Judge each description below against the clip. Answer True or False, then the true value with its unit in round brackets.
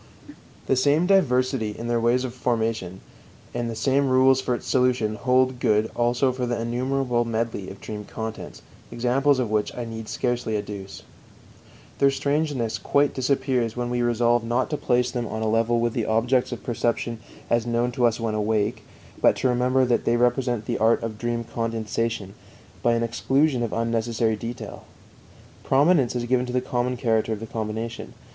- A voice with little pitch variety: True (2.1 semitones)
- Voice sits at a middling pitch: False (120 Hz)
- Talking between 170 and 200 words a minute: True (180 wpm)